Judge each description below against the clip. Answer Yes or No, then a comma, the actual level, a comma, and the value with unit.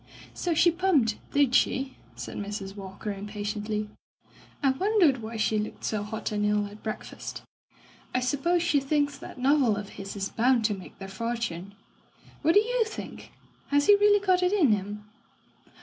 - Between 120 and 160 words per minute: No, average, 170 wpm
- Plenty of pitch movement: Yes, wide, 6.6 semitones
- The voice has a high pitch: Yes, high, 230 Hz